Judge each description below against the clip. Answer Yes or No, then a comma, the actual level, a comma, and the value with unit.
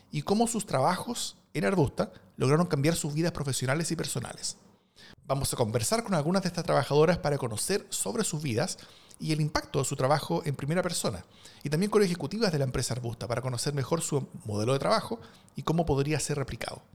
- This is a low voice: No, medium, 150 Hz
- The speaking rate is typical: No, fast, 195 wpm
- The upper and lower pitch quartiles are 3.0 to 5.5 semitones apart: Yes, average, 4.3 semitones